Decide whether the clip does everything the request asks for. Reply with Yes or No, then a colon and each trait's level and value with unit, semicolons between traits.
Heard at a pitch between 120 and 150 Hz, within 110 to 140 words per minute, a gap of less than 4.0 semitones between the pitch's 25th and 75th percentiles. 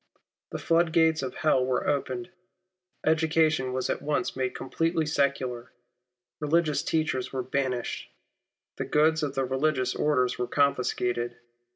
Yes: medium, 140 Hz; slow, 135 wpm; average, 3.5 semitones